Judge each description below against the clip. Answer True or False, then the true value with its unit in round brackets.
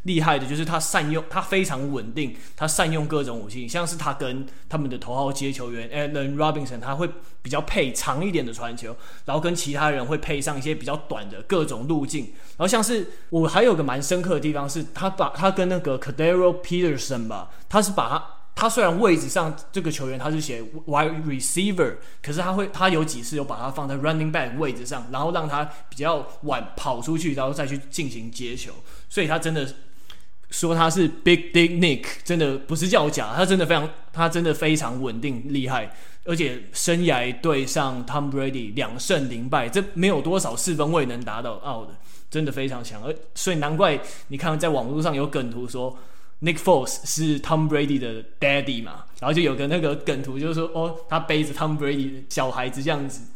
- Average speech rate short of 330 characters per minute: False (370 characters per minute)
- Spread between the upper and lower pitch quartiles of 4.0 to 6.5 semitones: False (3.6 semitones)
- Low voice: False (150 Hz)